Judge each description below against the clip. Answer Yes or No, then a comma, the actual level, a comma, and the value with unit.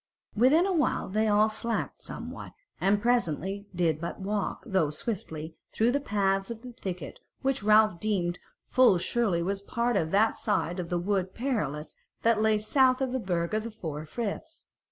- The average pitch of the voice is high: Yes, high, 205 Hz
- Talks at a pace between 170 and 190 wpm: Yes, average, 175 wpm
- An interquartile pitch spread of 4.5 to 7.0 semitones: Yes, average, 4.9 semitones